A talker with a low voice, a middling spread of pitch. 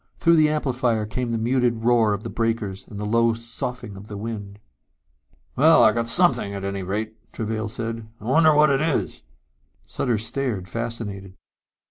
Yes: low, 115 Hz; average, 3.0 semitones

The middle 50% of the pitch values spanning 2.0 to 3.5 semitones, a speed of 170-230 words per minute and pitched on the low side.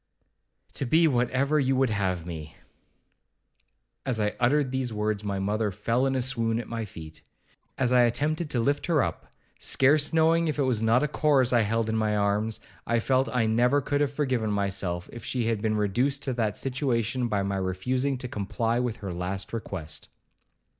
No: average, 4.2 semitones; average, 190 wpm; low, 120 Hz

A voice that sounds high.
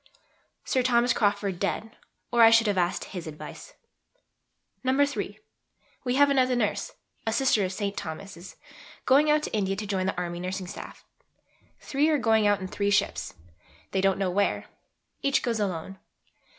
Yes: high, 205 Hz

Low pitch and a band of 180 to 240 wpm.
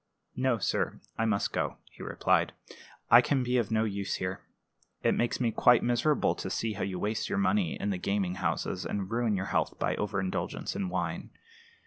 Yes: low, 110 Hz; average, 190 wpm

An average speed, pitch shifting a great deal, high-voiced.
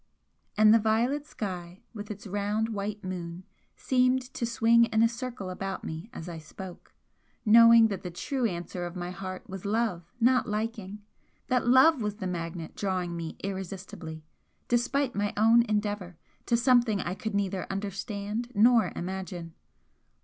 No: average, 155 wpm; average, 4.0 semitones; high, 205 Hz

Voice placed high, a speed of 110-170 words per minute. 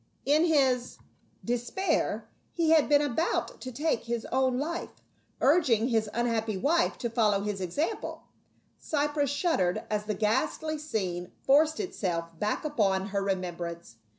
Yes: high, 240 Hz; average, 150 wpm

